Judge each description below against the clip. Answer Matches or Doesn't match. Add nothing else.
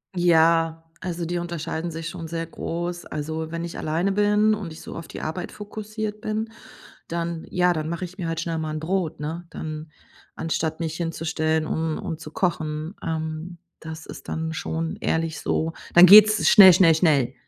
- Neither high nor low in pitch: Matches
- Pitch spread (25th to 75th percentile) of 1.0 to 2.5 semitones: Matches